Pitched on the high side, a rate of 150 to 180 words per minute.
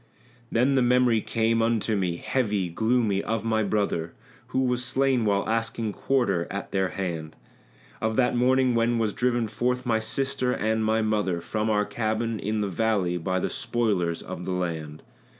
No: low, 110 Hz; average, 170 wpm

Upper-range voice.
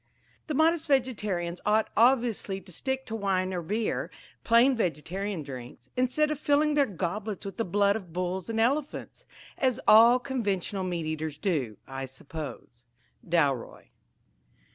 Yes: high, 200 Hz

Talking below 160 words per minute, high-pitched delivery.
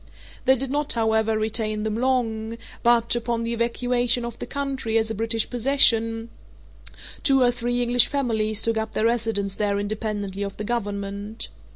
No: average, 165 wpm; high, 225 Hz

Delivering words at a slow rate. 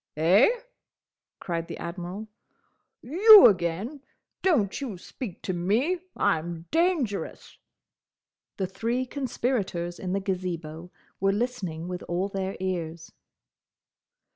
Yes: slow, 105 wpm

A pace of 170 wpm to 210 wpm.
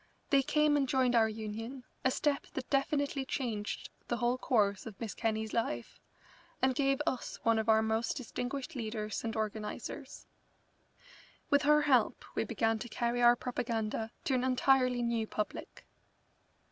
No: average, 155 wpm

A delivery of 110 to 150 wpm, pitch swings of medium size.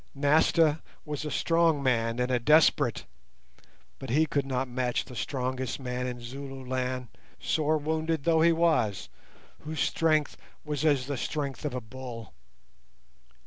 Yes: average, 145 wpm; average, 3.5 semitones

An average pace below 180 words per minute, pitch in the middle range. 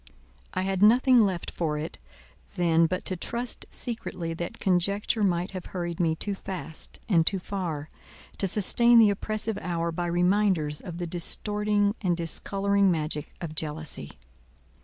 Yes: average, 150 wpm; medium, 180 Hz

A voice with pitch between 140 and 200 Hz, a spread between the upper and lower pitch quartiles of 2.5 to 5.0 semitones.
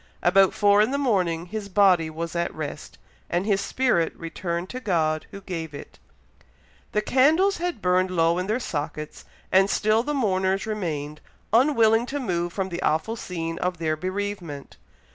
Yes: medium, 185 Hz; average, 4.5 semitones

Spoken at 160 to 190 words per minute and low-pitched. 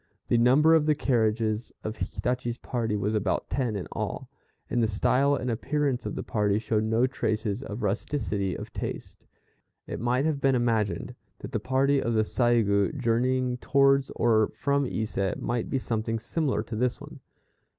Yes: average, 170 wpm; low, 120 Hz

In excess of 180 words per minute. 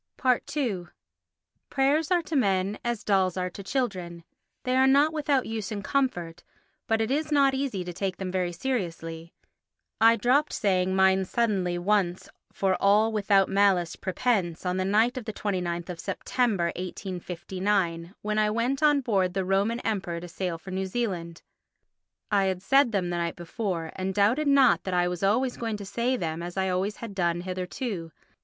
No: average, 175 wpm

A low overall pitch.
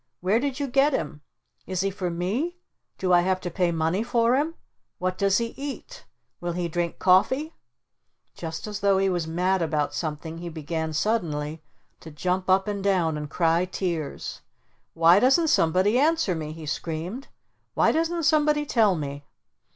No: medium, 185 Hz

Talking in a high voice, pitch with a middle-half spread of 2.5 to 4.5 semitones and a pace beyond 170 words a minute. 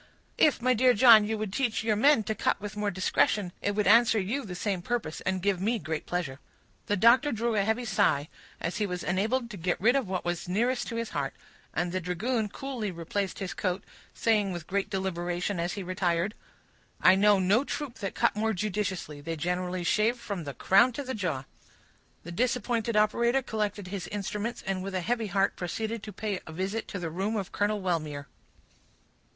Yes: high, 200 Hz; average, 3.8 semitones; average, 200 wpm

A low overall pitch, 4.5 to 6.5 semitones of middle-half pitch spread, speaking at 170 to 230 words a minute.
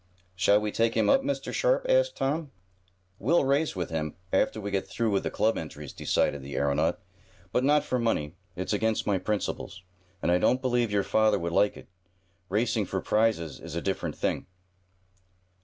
Yes: low, 105 Hz; wide, 5.6 semitones; average, 185 wpm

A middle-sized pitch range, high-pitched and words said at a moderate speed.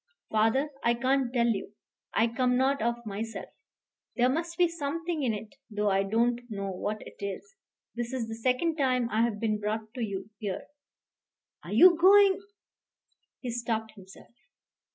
Yes: average, 3.9 semitones; high, 235 Hz; average, 170 wpm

